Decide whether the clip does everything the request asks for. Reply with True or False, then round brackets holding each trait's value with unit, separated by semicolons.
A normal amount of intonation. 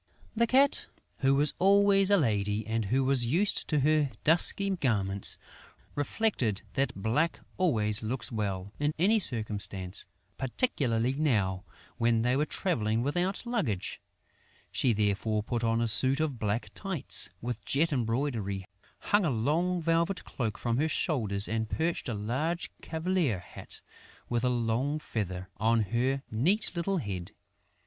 False (6.9 semitones)